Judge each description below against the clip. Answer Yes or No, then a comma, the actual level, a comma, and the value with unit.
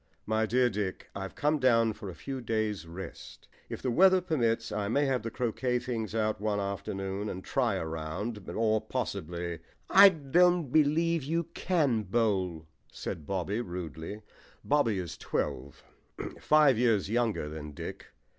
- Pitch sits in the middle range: No, low, 110 Hz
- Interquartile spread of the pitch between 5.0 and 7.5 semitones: Yes, wide, 5.5 semitones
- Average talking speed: Yes, average, 155 wpm